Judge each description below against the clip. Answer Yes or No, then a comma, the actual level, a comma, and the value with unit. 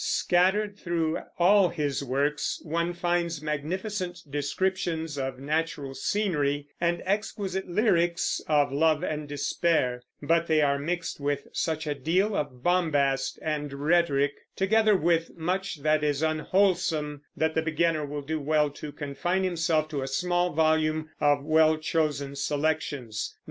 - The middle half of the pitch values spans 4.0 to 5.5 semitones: No, average, 3.2 semitones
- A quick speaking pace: No, average, 140 wpm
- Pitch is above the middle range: No, medium, 155 Hz